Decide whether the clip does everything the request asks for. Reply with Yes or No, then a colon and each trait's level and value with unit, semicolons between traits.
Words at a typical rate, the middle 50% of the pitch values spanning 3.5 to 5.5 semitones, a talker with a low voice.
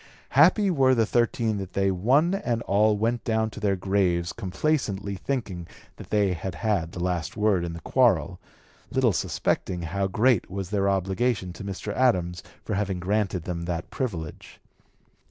Yes: average, 165 wpm; average, 4.0 semitones; low, 100 Hz